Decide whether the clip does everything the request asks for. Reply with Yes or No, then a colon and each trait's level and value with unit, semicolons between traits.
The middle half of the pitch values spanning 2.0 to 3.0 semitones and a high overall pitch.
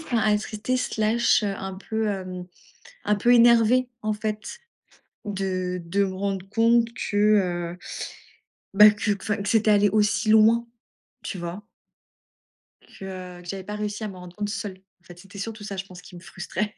Yes: narrow, 2.4 semitones; high, 205 Hz